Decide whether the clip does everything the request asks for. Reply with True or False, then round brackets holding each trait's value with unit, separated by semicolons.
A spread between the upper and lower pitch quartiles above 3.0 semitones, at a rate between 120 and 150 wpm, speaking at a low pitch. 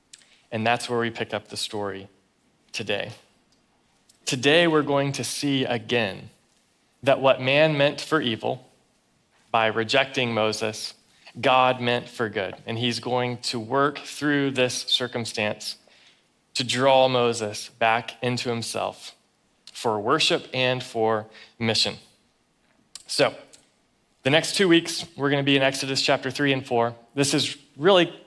True (3.5 semitones; 140 wpm; 125 Hz)